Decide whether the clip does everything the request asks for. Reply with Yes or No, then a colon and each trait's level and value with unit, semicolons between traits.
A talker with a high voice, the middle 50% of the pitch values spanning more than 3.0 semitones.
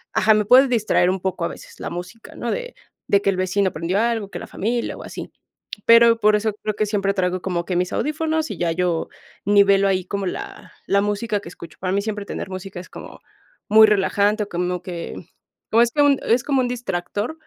Yes: high, 200 Hz; average, 3.7 semitones